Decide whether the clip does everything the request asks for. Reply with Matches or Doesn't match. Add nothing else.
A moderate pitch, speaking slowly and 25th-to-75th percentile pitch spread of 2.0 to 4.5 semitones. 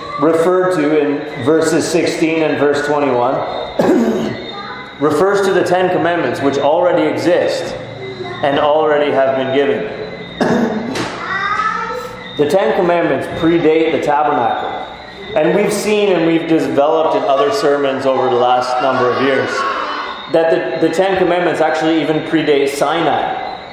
Matches